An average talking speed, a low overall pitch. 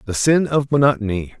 Yes: average, 170 wpm; low, 125 Hz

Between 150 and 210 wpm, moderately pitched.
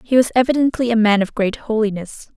No: average, 200 wpm; high, 225 Hz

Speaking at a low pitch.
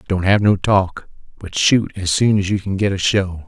Yes: very low, 95 Hz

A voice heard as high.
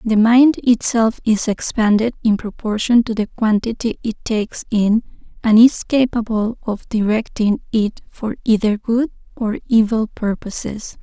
Yes: high, 220 Hz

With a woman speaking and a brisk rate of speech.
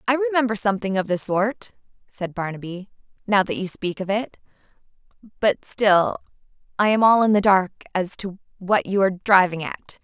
No: female; average, 175 wpm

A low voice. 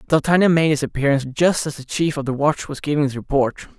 No: medium, 145 Hz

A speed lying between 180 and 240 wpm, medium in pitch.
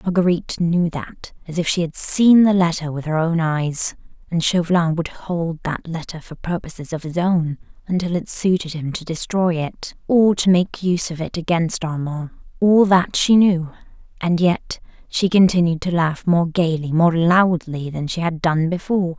Yes: average, 185 wpm; medium, 170 Hz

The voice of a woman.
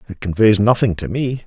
No: male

